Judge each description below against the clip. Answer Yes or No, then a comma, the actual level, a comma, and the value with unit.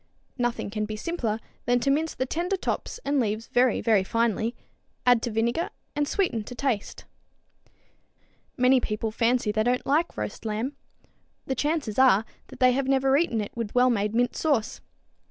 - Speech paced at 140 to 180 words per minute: Yes, average, 170 wpm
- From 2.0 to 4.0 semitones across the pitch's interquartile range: Yes, average, 3.7 semitones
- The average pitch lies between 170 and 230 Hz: No, high, 245 Hz